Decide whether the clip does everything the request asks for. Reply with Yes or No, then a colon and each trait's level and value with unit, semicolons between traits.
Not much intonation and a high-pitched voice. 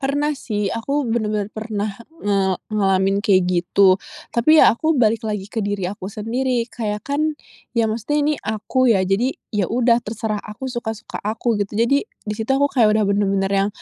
No: average, 3.1 semitones; high, 215 Hz